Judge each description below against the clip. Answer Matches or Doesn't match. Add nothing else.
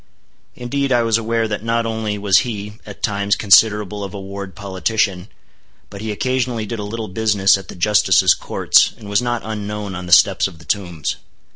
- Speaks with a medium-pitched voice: Doesn't match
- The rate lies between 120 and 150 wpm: Doesn't match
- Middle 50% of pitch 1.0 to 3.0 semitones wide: Matches